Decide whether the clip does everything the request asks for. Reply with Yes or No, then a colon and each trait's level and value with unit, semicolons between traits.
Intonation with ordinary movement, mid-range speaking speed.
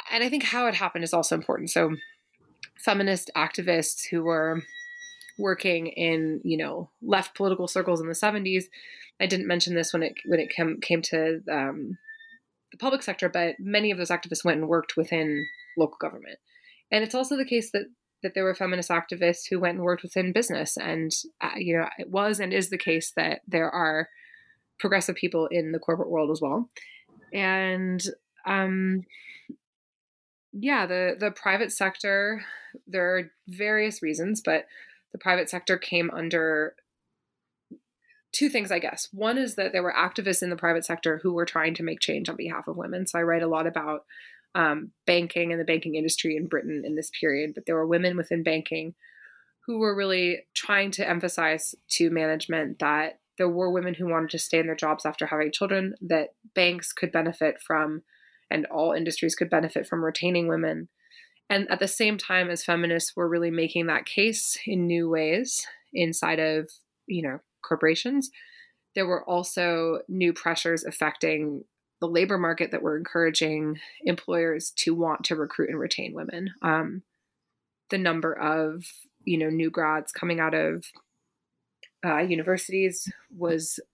Yes: average, 3.2 semitones; average, 170 wpm